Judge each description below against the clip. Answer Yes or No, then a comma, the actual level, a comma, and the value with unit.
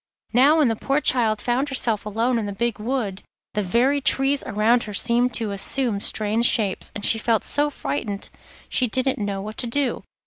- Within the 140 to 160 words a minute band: No, average, 195 wpm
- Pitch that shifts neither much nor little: Yes, average, 3.7 semitones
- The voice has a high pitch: Yes, high, 230 Hz